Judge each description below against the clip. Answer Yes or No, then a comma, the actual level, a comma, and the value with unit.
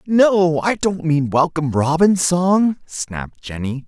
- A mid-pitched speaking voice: Yes, medium, 165 Hz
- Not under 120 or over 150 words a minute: Yes, average, 140 wpm